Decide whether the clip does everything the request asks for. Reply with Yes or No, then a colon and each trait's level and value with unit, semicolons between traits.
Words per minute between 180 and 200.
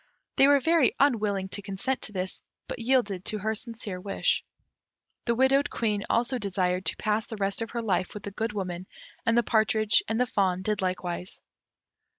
Yes: average, 185 wpm